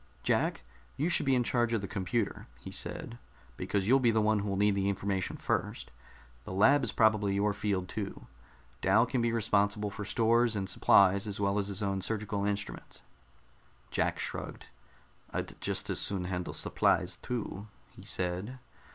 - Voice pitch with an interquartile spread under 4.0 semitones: Yes, average, 2.7 semitones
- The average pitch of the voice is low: Yes, low, 105 Hz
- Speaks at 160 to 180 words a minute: Yes, average, 170 wpm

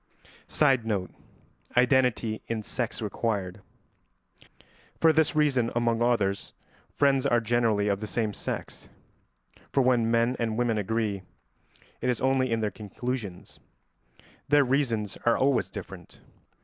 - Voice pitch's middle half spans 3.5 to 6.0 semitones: No, average, 3.1 semitones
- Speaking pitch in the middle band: No, low, 115 Hz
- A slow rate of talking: Yes, slow, 125 wpm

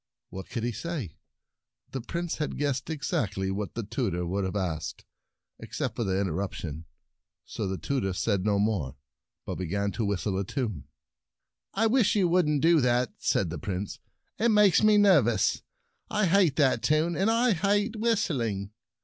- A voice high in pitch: No, low, 120 Hz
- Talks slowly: No, average, 170 wpm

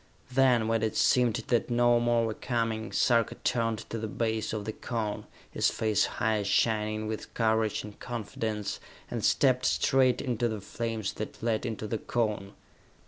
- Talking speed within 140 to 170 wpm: Yes, average, 165 wpm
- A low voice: Yes, low, 115 Hz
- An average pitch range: No, narrow, 1.7 semitones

